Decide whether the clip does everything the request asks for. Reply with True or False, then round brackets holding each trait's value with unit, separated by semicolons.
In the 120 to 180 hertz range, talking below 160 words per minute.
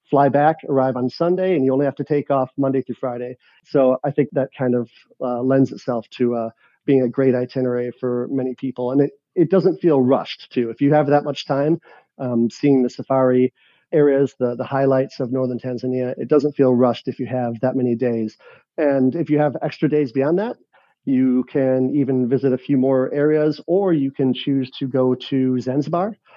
False (135 Hz; 205 wpm)